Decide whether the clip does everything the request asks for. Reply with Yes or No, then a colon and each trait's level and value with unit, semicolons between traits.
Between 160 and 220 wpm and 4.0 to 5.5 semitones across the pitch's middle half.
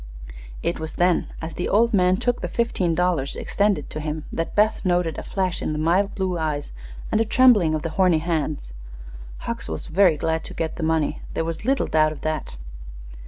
No: fast, 205 wpm; average, 3.5 semitones